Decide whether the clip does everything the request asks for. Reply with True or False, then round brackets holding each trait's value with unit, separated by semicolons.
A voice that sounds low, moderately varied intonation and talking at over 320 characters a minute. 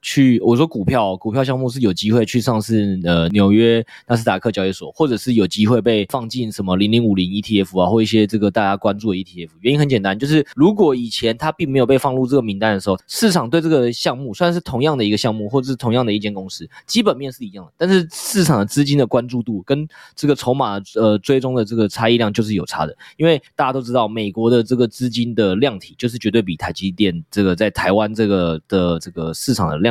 True (115 Hz; 4.5 semitones; 375 characters per minute)